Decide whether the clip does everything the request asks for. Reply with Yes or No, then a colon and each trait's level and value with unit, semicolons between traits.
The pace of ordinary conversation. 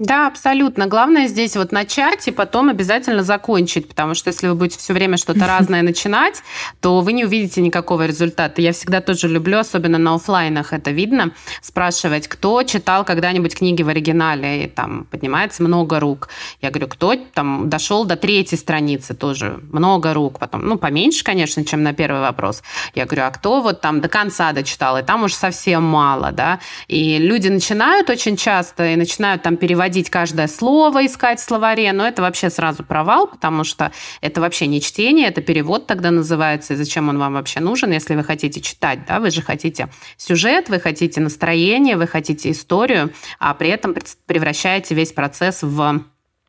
No: fast, 180 wpm